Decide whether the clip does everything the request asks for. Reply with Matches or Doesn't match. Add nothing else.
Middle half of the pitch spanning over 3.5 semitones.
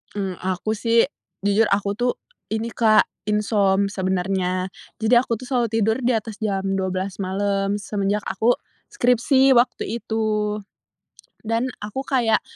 Doesn't match